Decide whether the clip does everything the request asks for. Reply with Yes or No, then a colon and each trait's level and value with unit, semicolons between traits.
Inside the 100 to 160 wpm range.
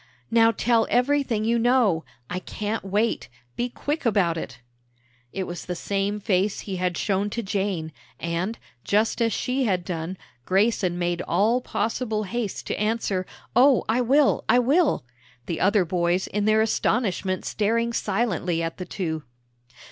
Yes: average, 155 wpm